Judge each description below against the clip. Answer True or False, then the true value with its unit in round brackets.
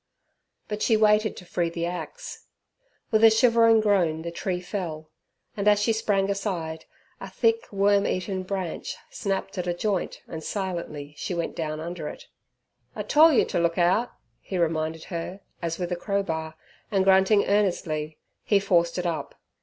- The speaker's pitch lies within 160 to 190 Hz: True (185 Hz)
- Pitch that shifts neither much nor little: True (3.5 semitones)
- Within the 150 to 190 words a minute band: True (170 wpm)